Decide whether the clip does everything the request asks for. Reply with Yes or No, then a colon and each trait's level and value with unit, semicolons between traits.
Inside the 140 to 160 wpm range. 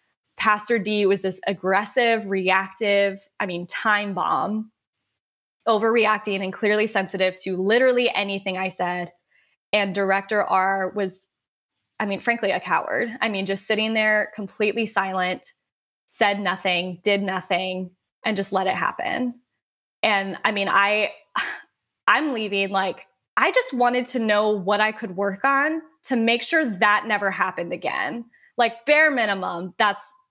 Yes: average, 145 wpm